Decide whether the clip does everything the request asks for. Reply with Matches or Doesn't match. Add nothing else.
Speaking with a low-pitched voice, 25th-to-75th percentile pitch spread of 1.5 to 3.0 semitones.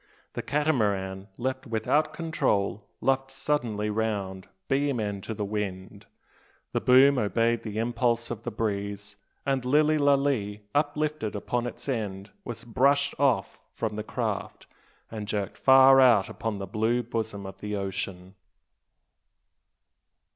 Doesn't match